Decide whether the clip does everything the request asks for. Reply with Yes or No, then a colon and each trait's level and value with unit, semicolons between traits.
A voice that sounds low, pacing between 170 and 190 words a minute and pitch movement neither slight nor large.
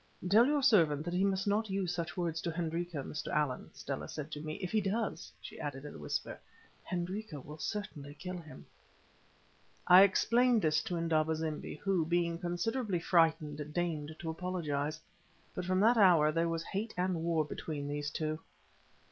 No: medium, 170 Hz; average, 175 wpm; average, 3.6 semitones